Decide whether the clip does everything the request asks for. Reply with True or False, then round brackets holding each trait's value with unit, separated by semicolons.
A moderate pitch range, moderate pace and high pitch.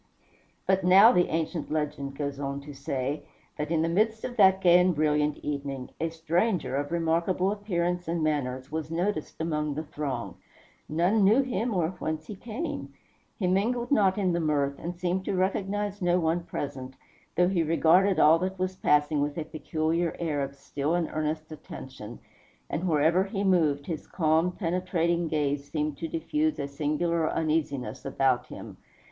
False (3.7 semitones; 170 wpm; 165 Hz)